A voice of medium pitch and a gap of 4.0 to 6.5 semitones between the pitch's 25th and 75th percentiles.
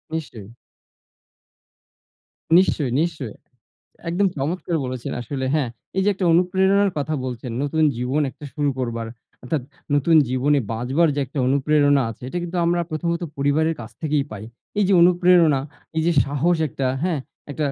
Yes: medium, 150 Hz; average, 4.5 semitones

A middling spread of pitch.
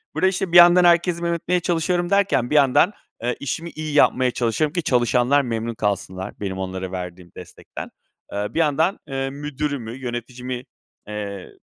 No: wide, 7.0 semitones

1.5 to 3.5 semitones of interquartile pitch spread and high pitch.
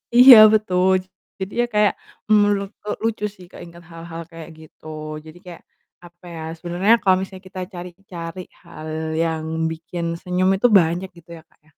No: narrow, 2.5 semitones; medium, 175 Hz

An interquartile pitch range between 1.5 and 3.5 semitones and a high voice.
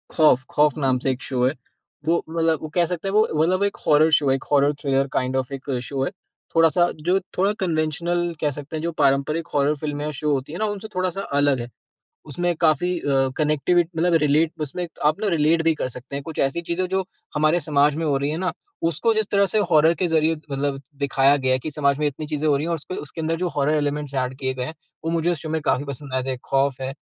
No: average, 3.2 semitones; medium, 150 Hz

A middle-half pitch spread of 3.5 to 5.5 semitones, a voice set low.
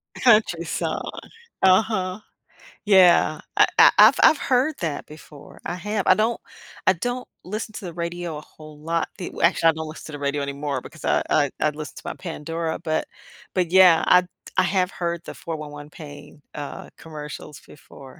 No: average, 3.8 semitones; medium, 165 Hz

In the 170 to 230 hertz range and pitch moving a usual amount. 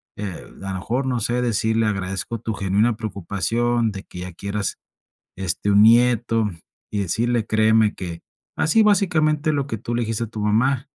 No: low, 110 Hz; average, 3.2 semitones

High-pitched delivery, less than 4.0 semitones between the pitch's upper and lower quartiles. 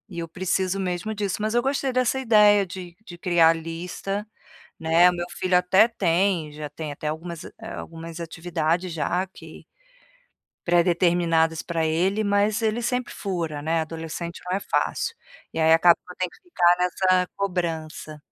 No: medium, 175 Hz; average, 3.1 semitones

